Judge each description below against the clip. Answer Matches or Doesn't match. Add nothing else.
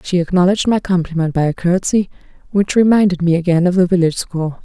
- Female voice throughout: Matches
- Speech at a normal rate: Matches